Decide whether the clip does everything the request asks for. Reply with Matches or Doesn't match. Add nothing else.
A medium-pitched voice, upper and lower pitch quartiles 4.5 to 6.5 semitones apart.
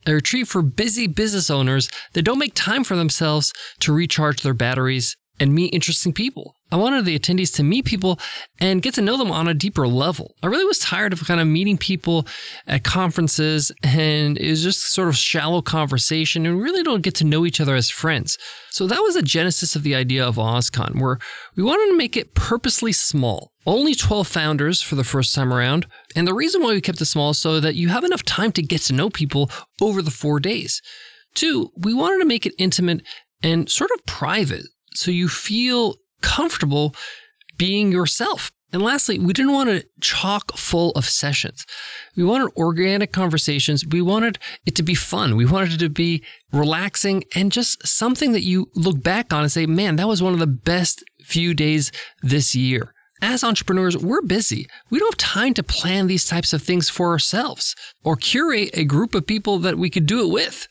Matches